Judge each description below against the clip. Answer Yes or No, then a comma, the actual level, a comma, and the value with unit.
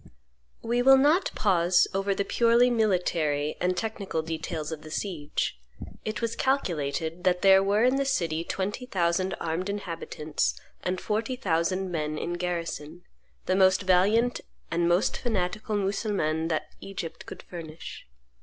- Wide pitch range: No, average, 4.4 semitones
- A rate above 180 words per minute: No, average, 145 wpm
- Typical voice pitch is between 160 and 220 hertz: Yes, medium, 185 Hz